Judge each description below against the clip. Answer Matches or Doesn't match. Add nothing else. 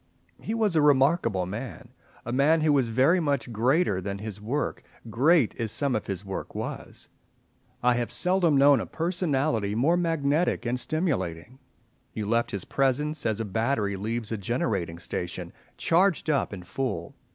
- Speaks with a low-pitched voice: Matches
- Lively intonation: Matches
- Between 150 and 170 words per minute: Matches